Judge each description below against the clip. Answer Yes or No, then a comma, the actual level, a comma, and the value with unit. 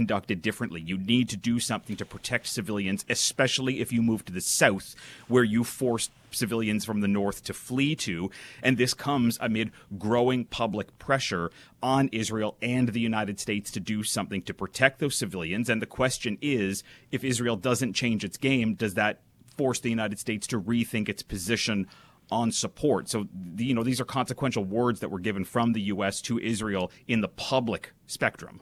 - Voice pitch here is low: Yes, low, 115 Hz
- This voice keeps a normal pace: Yes, average, 185 wpm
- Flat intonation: No, average, 3.1 semitones